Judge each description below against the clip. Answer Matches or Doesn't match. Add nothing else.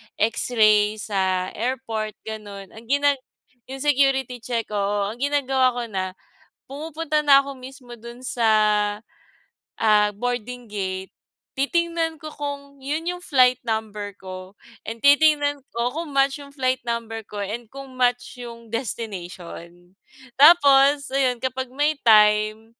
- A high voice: Matches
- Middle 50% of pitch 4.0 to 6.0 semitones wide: Matches